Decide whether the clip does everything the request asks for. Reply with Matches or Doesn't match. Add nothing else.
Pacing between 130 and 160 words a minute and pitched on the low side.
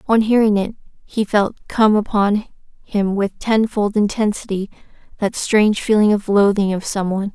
Doesn't match